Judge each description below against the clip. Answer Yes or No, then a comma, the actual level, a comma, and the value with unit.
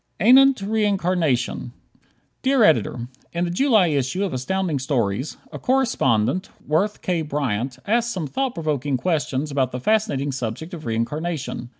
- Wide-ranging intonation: Yes, wide, 7.4 semitones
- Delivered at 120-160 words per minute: Yes, slow, 135 wpm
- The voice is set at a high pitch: No, medium, 155 Hz